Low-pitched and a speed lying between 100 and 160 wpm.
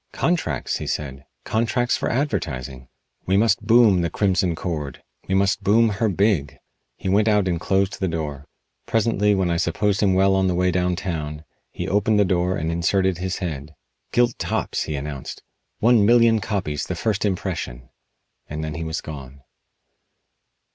No: very low, 95 Hz; average, 170 wpm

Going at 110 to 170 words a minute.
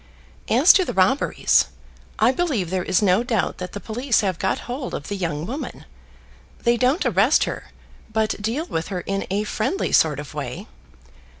No: average, 180 wpm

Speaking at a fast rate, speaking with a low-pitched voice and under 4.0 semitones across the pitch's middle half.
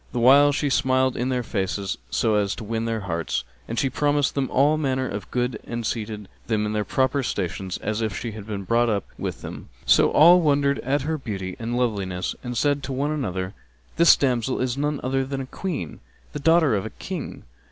No: fast, 215 wpm; low, 125 Hz; average, 4.8 semitones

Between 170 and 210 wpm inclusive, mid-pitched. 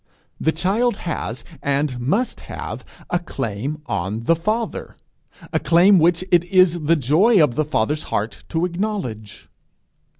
No: average, 140 wpm; medium, 160 Hz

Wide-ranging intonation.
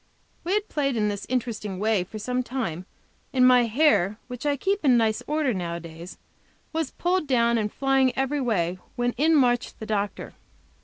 No: average, 4.7 semitones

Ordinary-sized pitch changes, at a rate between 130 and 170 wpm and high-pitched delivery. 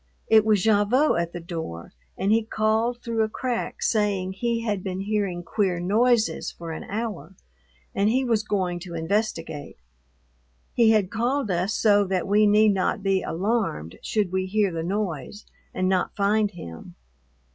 Yes: average, 3.2 semitones; average, 165 wpm; high, 205 Hz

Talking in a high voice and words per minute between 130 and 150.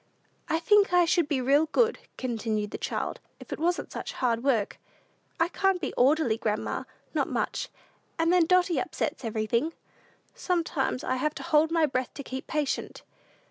No: very high, 300 Hz; average, 170 wpm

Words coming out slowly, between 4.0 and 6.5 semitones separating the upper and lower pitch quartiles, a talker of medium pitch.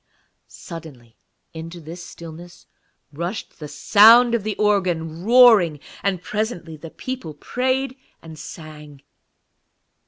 Yes: slow, 105 wpm; wide, 5.4 semitones; medium, 175 Hz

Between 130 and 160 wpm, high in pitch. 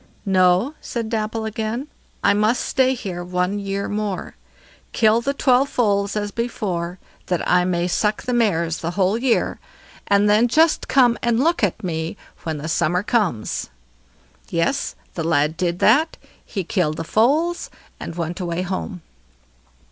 Yes: average, 155 wpm; high, 200 Hz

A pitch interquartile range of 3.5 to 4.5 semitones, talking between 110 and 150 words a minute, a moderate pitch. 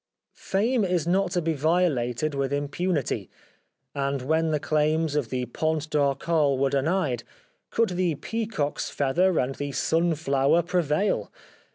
Yes: average, 4.0 semitones; average, 145 wpm; medium, 155 Hz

